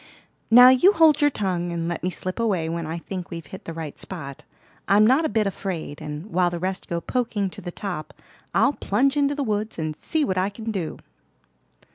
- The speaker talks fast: Yes, fast, 215 wpm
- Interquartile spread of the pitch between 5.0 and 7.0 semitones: Yes, wide, 5.4 semitones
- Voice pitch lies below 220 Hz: Yes, high, 190 Hz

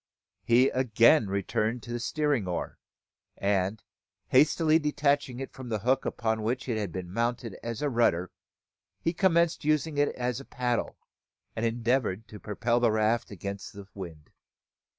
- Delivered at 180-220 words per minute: No, average, 155 wpm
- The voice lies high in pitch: No, low, 120 Hz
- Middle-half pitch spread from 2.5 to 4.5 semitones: Yes, average, 4.2 semitones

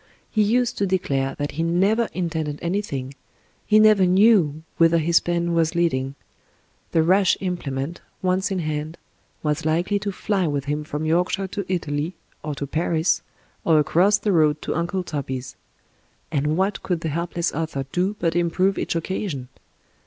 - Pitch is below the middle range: No, medium, 170 Hz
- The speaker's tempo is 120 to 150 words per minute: No, average, 165 wpm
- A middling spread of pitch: Yes, average, 3.8 semitones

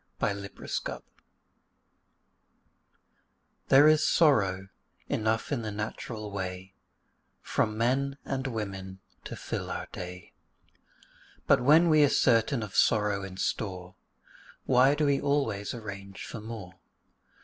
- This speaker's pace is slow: Yes, slow, 125 wpm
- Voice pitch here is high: No, low, 110 Hz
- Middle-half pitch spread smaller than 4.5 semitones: No, wide, 5.6 semitones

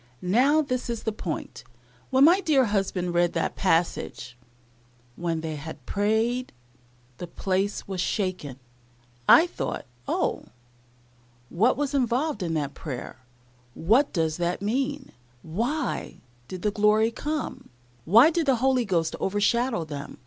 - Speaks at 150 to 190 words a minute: No, slow, 135 wpm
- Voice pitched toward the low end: No, high, 210 Hz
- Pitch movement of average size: No, wide, 7.1 semitones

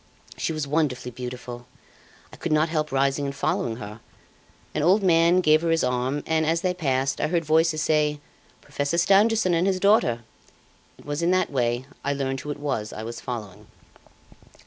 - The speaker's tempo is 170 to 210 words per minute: Yes, average, 185 wpm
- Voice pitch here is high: No, medium, 150 Hz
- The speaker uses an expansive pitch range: No, average, 4.6 semitones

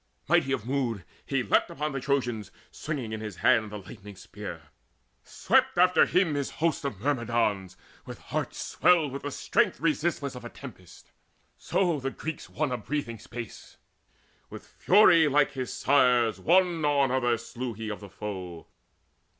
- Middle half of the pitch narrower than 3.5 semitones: No, average, 5.1 semitones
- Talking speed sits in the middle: Yes, average, 160 wpm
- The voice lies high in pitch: No, low, 130 Hz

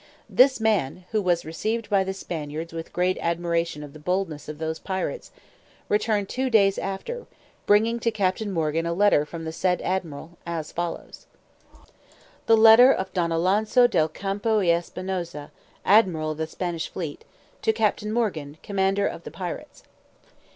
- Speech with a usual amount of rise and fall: Yes, average, 4.3 semitones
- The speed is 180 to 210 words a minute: No, average, 160 wpm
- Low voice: No, medium, 185 Hz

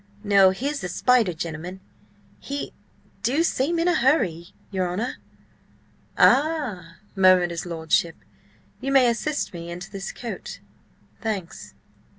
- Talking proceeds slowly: Yes, slow, 125 wpm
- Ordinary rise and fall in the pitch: No, wide, 7.2 semitones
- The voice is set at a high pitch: Yes, high, 195 Hz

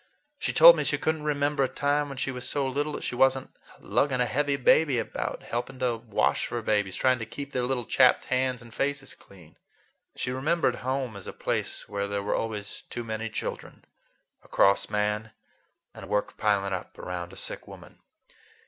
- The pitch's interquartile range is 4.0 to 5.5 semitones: Yes, average, 4.5 semitones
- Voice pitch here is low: Yes, low, 125 Hz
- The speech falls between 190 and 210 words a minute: Yes, average, 200 wpm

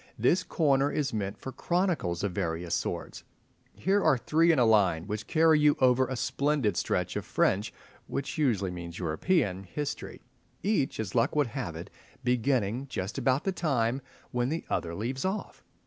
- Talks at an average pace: Yes, average, 170 wpm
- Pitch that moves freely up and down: Yes, wide, 7.0 semitones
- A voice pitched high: No, low, 125 Hz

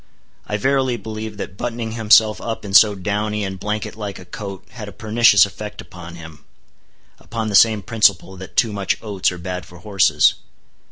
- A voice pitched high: No, low, 105 Hz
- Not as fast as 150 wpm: No, average, 180 wpm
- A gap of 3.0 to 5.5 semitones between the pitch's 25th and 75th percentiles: No, narrow, 2.6 semitones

